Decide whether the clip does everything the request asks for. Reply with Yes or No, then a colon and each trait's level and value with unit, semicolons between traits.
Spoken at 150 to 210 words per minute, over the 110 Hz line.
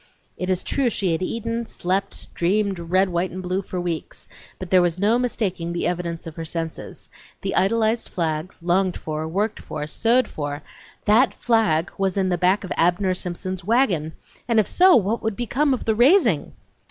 Yes: average, 185 wpm; medium, 185 Hz